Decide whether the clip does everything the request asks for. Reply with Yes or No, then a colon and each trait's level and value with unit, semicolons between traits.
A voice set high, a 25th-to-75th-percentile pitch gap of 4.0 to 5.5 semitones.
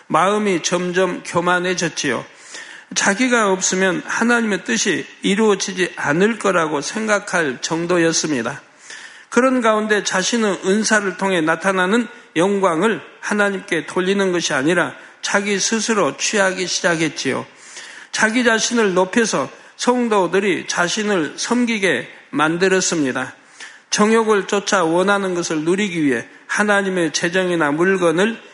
No: high, 195 Hz; average, 3.2 semitones